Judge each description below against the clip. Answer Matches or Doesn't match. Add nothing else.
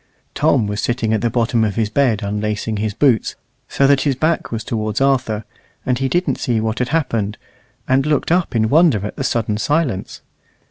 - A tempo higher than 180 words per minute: Matches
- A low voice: Matches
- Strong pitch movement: Doesn't match